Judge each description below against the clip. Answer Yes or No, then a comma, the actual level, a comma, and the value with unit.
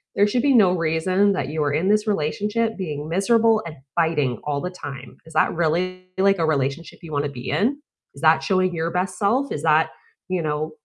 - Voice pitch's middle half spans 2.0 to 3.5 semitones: No, average, 4.5 semitones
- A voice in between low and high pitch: Yes, medium, 175 Hz